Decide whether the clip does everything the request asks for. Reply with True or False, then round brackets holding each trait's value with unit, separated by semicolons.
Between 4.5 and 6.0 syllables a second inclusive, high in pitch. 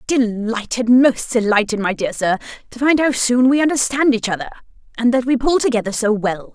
True (5.4 syllables/s; 240 Hz)